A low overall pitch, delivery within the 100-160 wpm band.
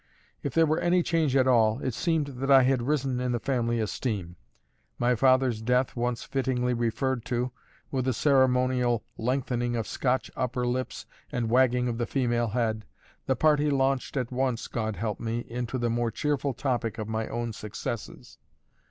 No: low, 125 Hz; average, 175 wpm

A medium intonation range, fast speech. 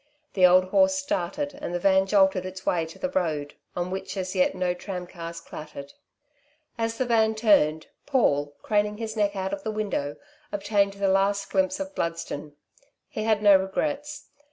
No: average, 3.5 semitones; average, 175 wpm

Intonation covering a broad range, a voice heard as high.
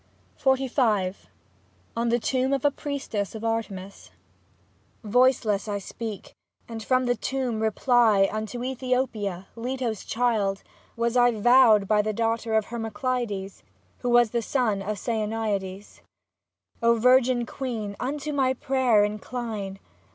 No: average, 3.3 semitones; high, 230 Hz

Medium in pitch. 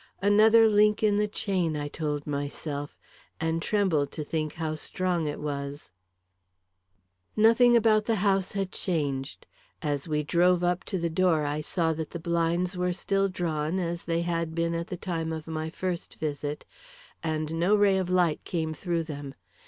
Yes: medium, 170 Hz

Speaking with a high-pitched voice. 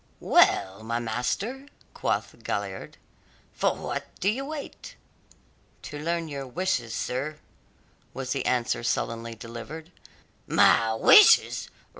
No: low, 135 Hz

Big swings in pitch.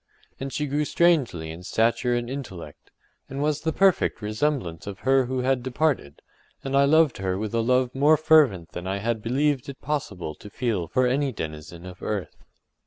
Yes: wide, 6.5 semitones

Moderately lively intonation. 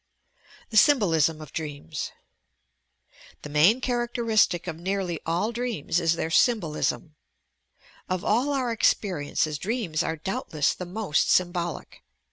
No: wide, 5.8 semitones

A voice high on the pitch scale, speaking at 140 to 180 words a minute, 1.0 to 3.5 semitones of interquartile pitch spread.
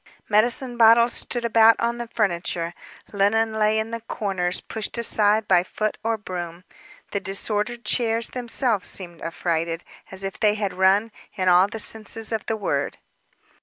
Yes: high, 215 Hz; average, 160 wpm; average, 3.2 semitones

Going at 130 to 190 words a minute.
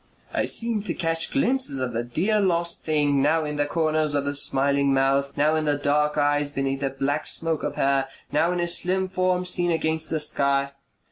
No: average, 200 wpm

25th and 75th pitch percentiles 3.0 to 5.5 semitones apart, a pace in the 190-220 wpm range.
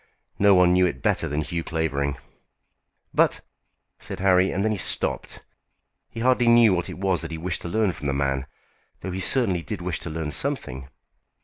Yes: average, 3.7 semitones; average, 200 wpm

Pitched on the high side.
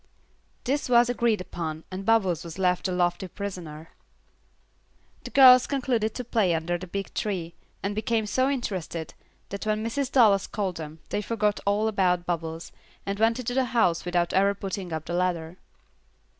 Yes: high, 195 Hz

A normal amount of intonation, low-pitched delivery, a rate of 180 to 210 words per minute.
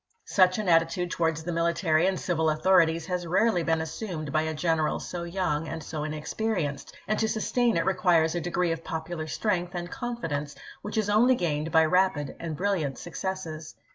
No: average, 3.0 semitones; medium, 170 Hz; average, 190 wpm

